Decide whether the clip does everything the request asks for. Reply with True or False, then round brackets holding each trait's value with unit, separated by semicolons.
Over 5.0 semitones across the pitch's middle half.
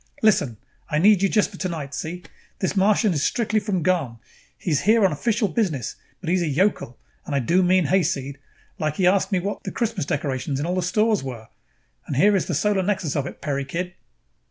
True (5.6 semitones)